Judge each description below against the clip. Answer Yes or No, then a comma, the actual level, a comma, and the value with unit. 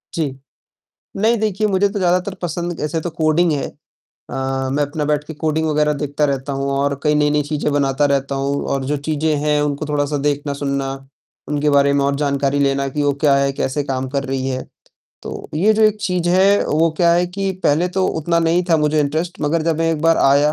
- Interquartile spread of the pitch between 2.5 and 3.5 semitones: Yes, average, 2.9 semitones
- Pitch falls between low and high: Yes, medium, 150 Hz